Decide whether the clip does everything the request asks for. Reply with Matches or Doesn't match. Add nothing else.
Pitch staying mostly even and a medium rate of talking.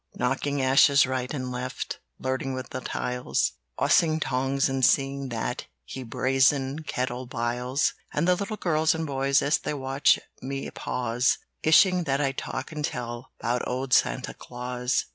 Matches